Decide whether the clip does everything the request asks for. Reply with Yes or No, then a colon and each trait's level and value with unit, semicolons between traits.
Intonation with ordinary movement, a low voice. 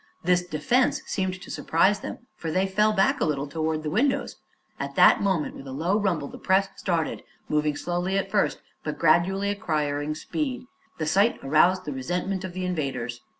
No: average, 4.3 semitones; medium, 180 Hz